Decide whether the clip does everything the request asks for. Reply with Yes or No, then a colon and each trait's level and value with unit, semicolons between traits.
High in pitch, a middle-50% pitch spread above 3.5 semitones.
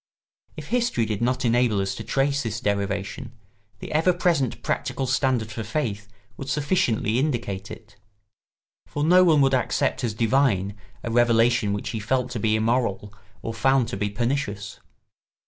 No: low, 120 Hz; average, 4.4 semitones